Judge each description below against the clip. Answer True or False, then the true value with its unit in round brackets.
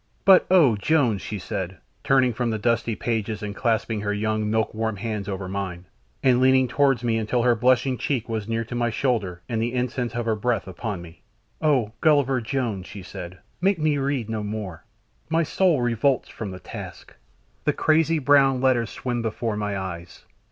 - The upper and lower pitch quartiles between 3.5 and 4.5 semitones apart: True (3.9 semitones)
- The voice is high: False (115 Hz)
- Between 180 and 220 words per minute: True (185 wpm)